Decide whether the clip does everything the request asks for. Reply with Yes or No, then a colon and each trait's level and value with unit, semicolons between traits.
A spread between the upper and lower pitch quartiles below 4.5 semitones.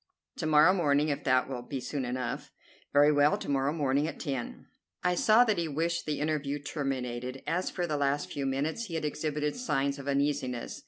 Yes: narrow, 2.4 semitones